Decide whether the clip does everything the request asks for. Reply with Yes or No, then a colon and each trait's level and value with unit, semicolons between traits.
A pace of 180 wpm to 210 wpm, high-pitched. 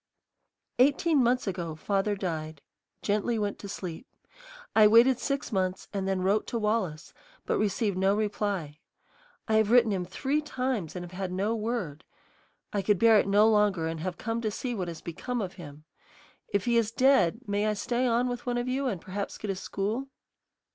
Yes: average, 190 wpm; high, 210 Hz